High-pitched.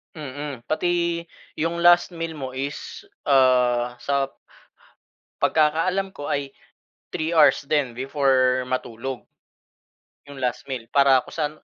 No: medium, 140 Hz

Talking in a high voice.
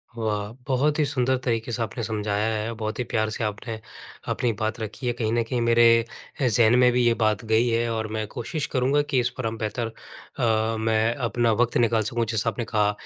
No: low, 115 Hz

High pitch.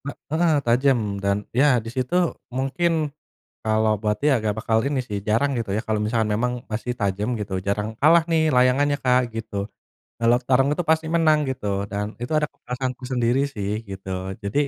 No: low, 125 Hz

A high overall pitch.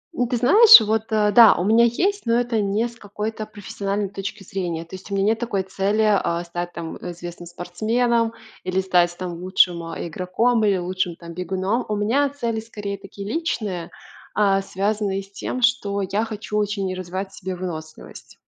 Yes: high, 200 Hz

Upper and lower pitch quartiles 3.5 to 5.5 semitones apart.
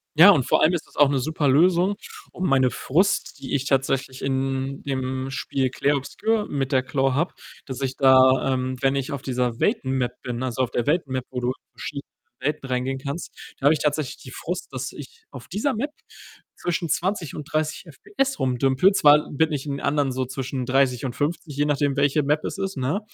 No: average, 2.9 semitones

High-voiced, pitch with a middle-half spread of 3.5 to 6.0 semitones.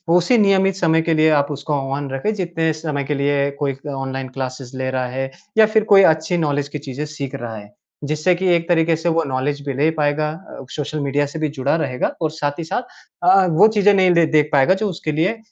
No: medium, 150 Hz; average, 3.8 semitones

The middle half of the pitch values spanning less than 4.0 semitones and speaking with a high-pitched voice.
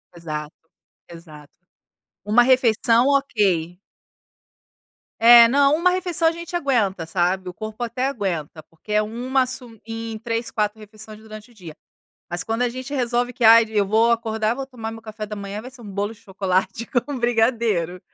Yes: average, 3.6 semitones; high, 225 Hz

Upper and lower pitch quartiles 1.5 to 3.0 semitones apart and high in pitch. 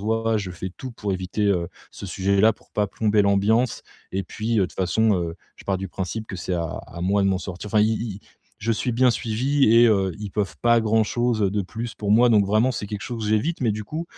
No: narrow, 2.6 semitones; low, 105 Hz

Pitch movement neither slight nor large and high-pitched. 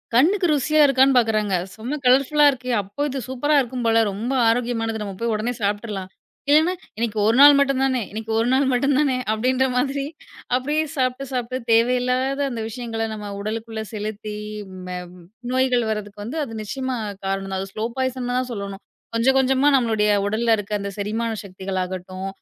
Yes: average, 3.7 semitones; high, 235 Hz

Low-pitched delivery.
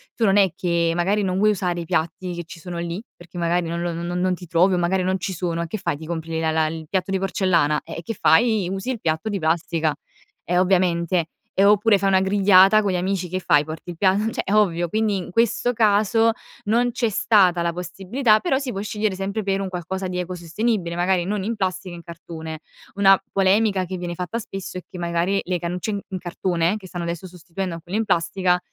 No: medium, 185 Hz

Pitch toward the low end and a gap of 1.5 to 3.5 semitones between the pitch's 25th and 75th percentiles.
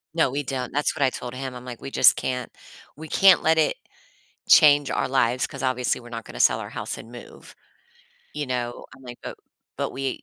Yes: low, 130 Hz; narrow, 2.6 semitones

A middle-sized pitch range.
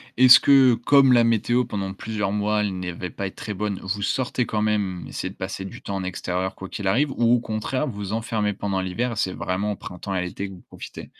Yes: average, 3.5 semitones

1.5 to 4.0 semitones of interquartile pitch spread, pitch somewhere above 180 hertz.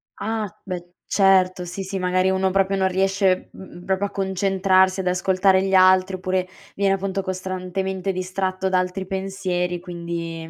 No: narrow, 0.9 semitones; high, 190 Hz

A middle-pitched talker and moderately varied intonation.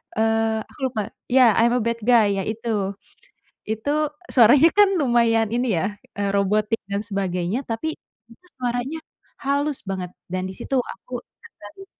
No: high, 225 Hz; average, 3.6 semitones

